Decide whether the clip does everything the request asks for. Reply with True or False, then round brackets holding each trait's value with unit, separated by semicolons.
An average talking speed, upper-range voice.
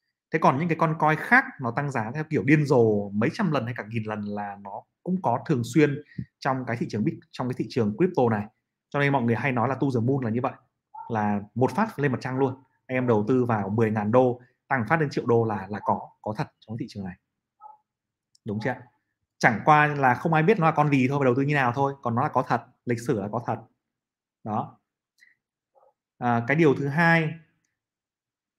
False (240 wpm; 130 Hz)